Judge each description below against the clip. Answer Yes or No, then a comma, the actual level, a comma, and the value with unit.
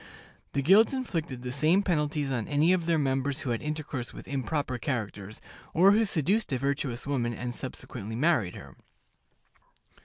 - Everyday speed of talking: Yes, average, 160 wpm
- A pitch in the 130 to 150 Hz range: Yes, medium, 140 Hz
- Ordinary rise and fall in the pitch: Yes, average, 4.9 semitones